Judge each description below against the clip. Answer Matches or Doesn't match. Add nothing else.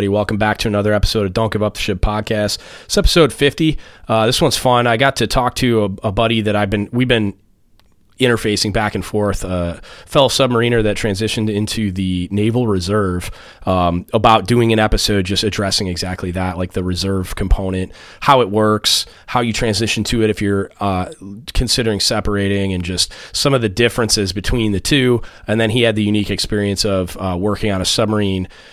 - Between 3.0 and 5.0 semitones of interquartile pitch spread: Doesn't match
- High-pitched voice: Doesn't match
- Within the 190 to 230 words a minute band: Matches